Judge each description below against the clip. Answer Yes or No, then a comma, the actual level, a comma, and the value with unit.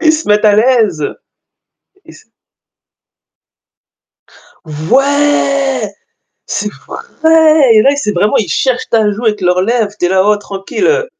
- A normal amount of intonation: No, wide, 5.7 semitones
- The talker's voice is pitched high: Yes, high, 225 Hz